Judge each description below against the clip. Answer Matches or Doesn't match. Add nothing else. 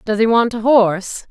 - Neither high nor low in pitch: Doesn't match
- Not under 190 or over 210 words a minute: Doesn't match